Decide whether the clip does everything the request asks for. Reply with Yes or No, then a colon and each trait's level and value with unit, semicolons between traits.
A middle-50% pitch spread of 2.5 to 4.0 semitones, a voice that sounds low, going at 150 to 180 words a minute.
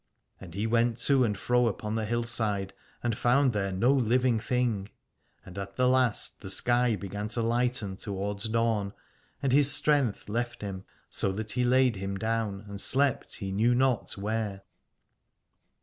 Yes: average, 3.5 semitones; low, 115 Hz; average, 165 wpm